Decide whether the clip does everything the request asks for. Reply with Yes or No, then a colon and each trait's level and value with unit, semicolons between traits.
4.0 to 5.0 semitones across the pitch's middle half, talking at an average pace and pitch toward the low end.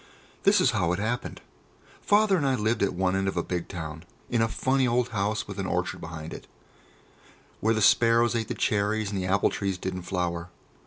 No: average, 4.3 semitones; fast, 210 wpm; low, 100 Hz